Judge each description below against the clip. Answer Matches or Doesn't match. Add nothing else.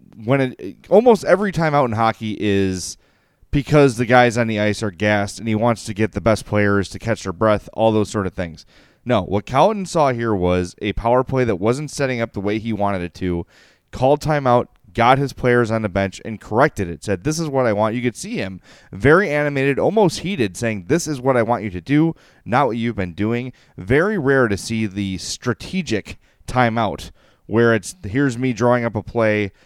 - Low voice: Matches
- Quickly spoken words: Matches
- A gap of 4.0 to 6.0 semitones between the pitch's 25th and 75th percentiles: Matches